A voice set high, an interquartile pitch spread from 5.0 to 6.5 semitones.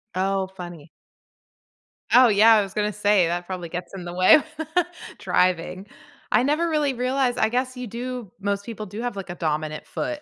Yes: high, 200 Hz; average, 5.3 semitones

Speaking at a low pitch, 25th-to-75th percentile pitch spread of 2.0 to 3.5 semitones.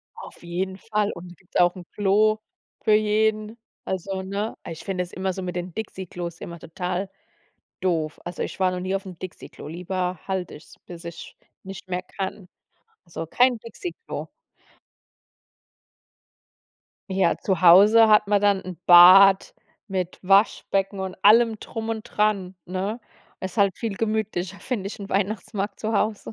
No: high, 190 Hz; average, 2.8 semitones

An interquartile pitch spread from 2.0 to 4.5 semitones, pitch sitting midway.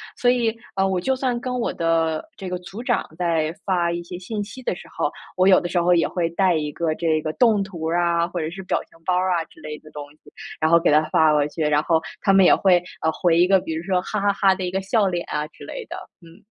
Yes: average, 2.8 semitones; medium, 175 Hz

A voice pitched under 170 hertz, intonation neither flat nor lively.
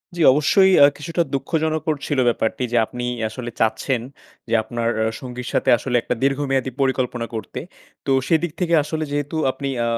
Yes: low, 135 Hz; average, 4.2 semitones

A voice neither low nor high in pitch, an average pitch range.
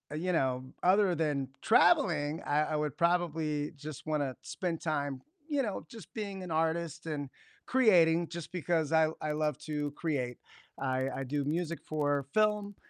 Yes: medium, 155 Hz; average, 3.2 semitones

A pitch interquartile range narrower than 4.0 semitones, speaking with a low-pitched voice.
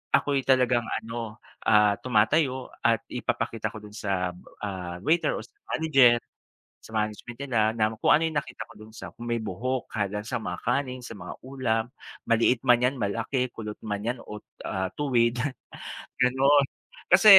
Yes: average, 3.4 semitones; low, 115 Hz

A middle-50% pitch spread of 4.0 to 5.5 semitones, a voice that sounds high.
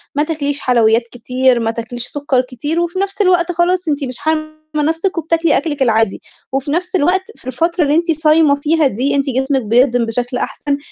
Yes: average, 4.6 semitones; very high, 290 Hz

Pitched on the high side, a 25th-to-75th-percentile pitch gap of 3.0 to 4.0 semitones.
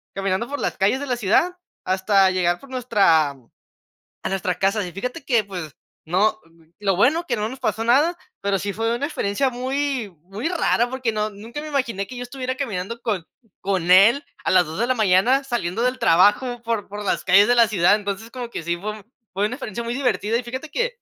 No: high, 220 Hz; average, 4.6 semitones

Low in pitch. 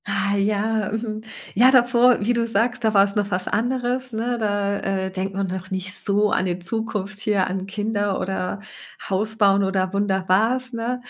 No: high, 205 Hz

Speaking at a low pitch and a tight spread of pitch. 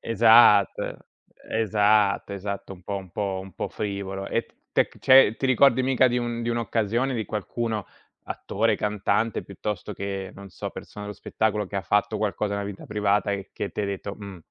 Yes: low, 105 Hz; narrow, 2.2 semitones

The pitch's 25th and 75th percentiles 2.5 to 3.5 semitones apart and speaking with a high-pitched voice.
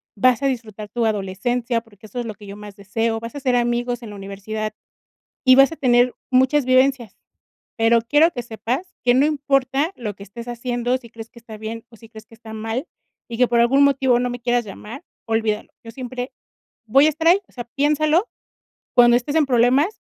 Yes: average, 2.8 semitones; high, 240 Hz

